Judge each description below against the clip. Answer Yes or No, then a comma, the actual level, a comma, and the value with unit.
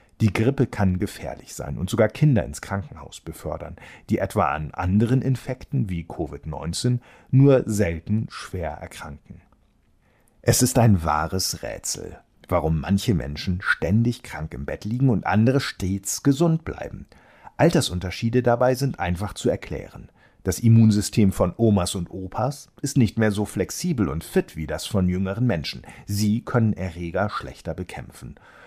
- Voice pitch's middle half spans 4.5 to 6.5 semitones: Yes, average, 5.3 semitones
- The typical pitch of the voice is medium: No, low, 105 Hz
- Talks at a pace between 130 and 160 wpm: Yes, average, 145 wpm